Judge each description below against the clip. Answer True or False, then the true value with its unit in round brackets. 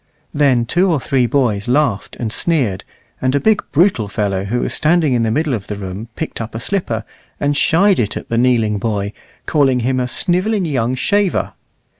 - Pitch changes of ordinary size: False (5.9 semitones)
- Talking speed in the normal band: True (195 wpm)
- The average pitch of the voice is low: True (125 Hz)